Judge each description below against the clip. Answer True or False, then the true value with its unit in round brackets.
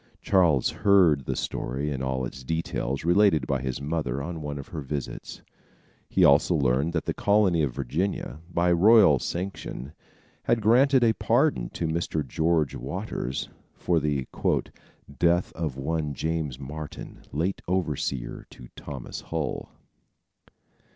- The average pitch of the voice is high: False (75 Hz)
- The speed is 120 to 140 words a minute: True (135 wpm)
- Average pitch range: True (4.3 semitones)